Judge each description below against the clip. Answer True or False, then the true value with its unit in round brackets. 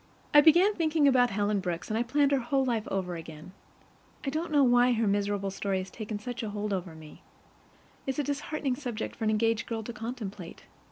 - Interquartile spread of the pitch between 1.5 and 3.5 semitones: False (5.1 semitones)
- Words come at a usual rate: False (210 wpm)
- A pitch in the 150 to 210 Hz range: False (230 Hz)